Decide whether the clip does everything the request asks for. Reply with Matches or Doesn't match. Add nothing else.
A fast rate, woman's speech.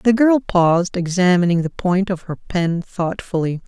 Doesn't match